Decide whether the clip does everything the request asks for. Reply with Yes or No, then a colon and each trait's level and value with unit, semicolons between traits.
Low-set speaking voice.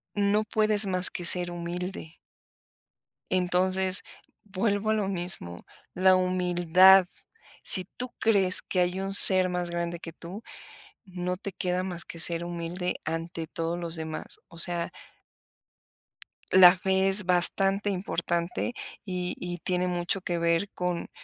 No: medium, 180 Hz